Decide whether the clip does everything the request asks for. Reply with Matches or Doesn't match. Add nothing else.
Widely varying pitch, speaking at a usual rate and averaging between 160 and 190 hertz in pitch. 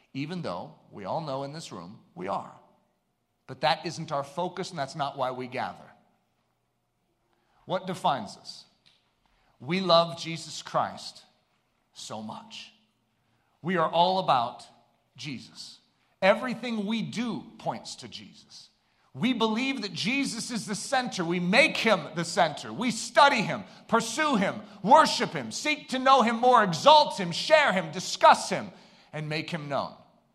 Matches